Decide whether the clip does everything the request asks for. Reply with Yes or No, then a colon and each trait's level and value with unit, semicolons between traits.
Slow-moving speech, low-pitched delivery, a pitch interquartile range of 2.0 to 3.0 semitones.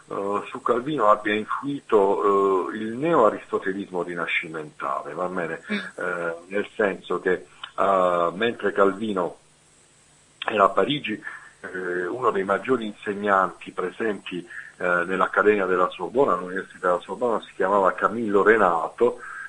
Yes: slow, 100 wpm; low, 100 Hz; average, 2.7 semitones